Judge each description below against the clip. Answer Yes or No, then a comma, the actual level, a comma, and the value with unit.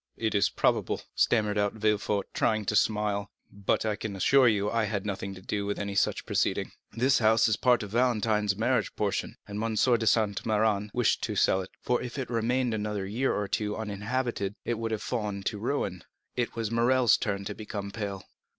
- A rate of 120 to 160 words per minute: No, fast, 205 wpm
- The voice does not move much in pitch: Yes, narrow, 2.2 semitones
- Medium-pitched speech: No, low, 105 Hz